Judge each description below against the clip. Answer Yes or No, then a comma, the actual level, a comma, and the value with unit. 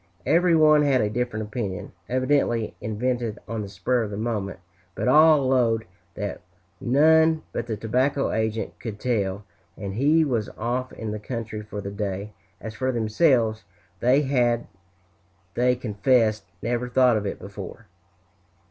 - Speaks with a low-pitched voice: Yes, low, 115 Hz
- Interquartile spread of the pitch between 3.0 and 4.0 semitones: Yes, average, 3.3 semitones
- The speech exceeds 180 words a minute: No, average, 150 wpm